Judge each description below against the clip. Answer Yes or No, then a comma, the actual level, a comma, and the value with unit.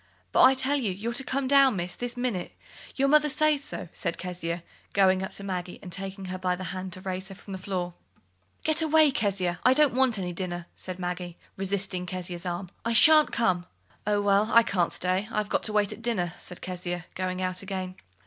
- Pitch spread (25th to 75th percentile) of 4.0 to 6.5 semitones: Yes, average, 4.6 semitones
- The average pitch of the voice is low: No, high, 190 Hz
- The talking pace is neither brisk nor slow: No, fast, 215 wpm